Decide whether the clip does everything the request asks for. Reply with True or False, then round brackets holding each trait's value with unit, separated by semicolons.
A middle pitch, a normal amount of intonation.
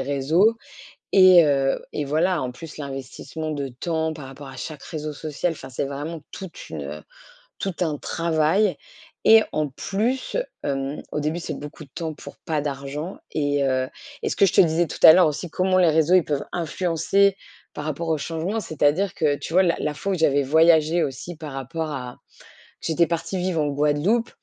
True (155 Hz; 3.3 semitones)